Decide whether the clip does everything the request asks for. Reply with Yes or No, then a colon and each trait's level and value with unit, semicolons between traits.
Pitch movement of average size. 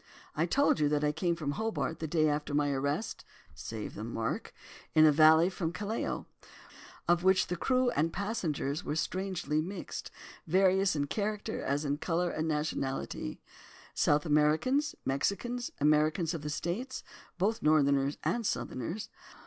Yes: average, 4.6 semitones